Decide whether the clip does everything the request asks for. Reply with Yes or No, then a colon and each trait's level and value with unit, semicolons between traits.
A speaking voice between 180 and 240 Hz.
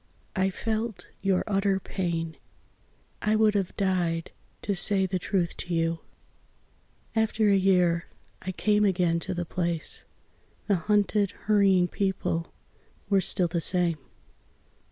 Yes: high, 190 Hz